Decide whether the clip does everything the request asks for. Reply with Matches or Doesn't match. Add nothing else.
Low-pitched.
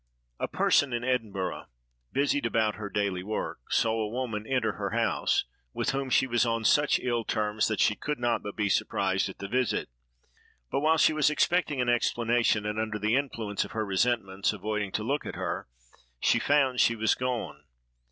Matches